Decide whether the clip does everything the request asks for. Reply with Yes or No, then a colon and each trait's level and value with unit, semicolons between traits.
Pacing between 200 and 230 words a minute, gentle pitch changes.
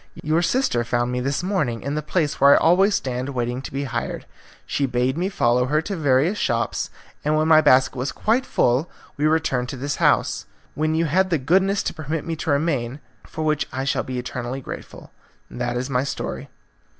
No: fast, 205 wpm; average, 4.3 semitones